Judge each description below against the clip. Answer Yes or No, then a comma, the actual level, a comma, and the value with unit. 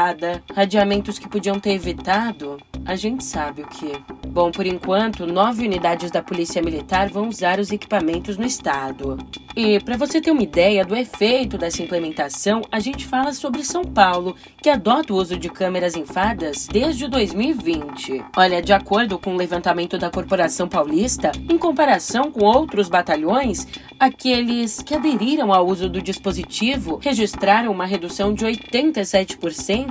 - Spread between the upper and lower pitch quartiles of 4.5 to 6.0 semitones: Yes, average, 4.9 semitones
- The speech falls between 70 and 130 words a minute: No, average, 150 wpm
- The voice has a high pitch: Yes, high, 200 Hz